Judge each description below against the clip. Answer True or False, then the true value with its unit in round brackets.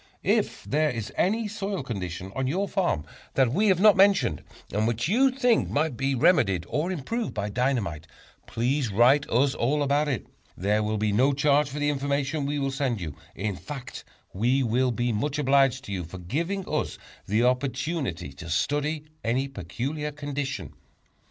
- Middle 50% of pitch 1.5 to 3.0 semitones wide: False (5.1 semitones)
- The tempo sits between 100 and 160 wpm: False (175 wpm)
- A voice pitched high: False (135 Hz)